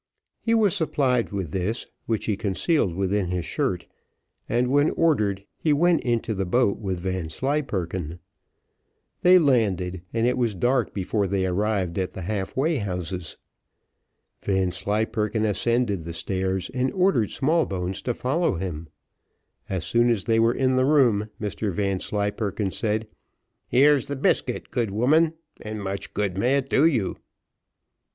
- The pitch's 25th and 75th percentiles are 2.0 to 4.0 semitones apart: No, average, 5.2 semitones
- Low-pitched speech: Yes, low, 105 Hz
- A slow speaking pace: No, average, 145 wpm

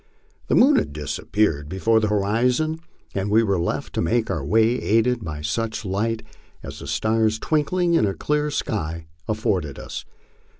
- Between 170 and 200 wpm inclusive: Yes, average, 175 wpm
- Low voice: Yes, low, 110 Hz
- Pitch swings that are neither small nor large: Yes, average, 3.9 semitones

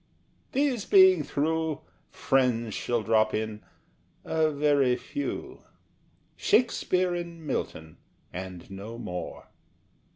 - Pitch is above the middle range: No, low, 135 Hz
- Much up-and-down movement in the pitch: Yes, wide, 7.9 semitones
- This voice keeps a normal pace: No, slow, 95 wpm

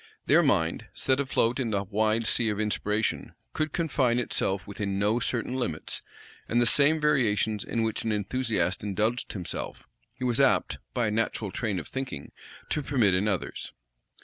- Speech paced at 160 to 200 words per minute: Yes, average, 170 wpm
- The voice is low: Yes, low, 110 Hz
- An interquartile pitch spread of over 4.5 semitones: No, average, 3.8 semitones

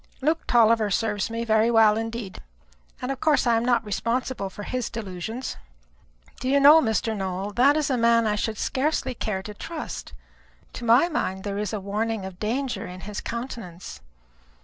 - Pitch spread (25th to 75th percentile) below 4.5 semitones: Yes, average, 3.4 semitones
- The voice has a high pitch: Yes, high, 225 Hz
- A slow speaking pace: No, average, 180 wpm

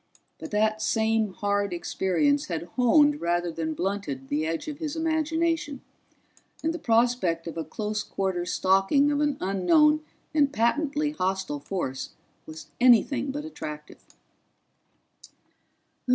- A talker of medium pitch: No, high, 215 Hz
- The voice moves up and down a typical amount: No, wide, 8.7 semitones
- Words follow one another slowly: Yes, slow, 125 wpm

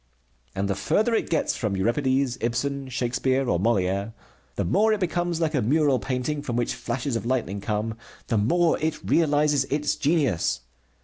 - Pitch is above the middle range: No, low, 130 Hz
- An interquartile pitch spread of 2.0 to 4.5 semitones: No, average, 4.9 semitones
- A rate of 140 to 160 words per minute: No, average, 170 wpm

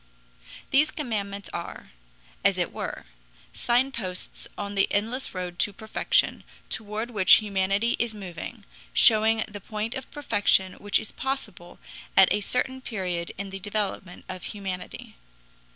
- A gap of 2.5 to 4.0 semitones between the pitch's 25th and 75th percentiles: Yes, average, 3.2 semitones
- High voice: Yes, high, 205 Hz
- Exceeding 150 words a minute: No, slow, 135 wpm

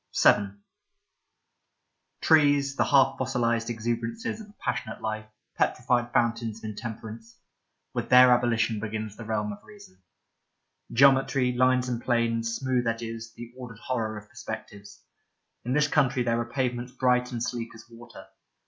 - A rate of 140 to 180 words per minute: Yes, average, 155 wpm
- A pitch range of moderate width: No, narrow, 2.0 semitones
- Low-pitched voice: Yes, low, 120 Hz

